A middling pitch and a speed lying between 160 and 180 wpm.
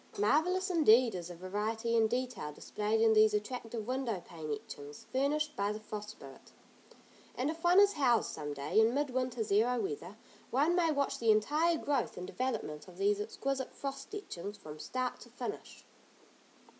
No: high, 230 Hz; average, 170 wpm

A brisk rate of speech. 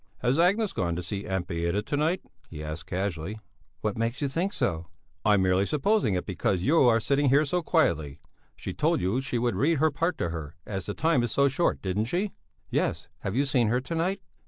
Yes: fast, 220 wpm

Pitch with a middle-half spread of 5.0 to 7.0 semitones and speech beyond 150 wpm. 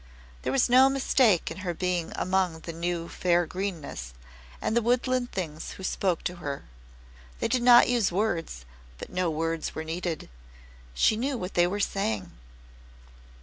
Yes: average, 5.3 semitones; average, 160 wpm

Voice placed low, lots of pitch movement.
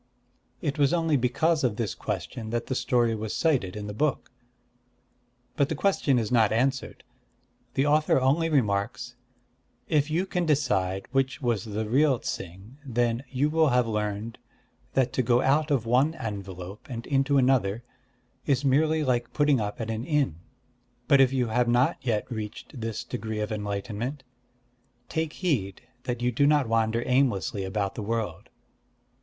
No: low, 125 Hz; average, 4.6 semitones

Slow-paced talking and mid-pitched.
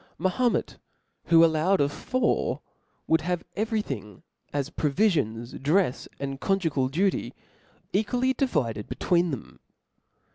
Yes: slow, 115 wpm; medium, 165 Hz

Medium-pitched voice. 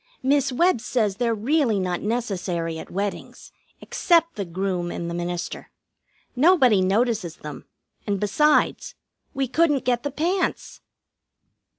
No: high, 220 Hz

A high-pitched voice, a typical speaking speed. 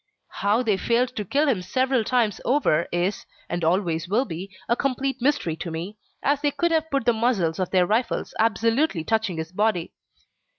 Yes: high, 220 Hz; average, 185 wpm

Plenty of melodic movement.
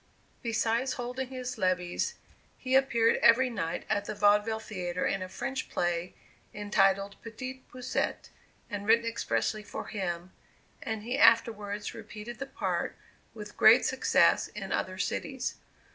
No: average, 3.7 semitones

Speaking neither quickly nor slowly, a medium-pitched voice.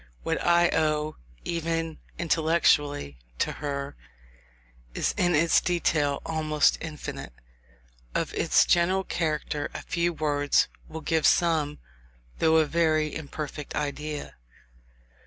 No: slow, 110 wpm; medium, 155 Hz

